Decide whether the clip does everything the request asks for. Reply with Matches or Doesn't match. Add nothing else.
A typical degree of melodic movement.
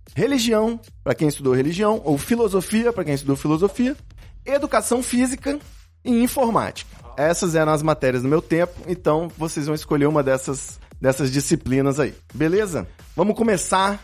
Doesn't match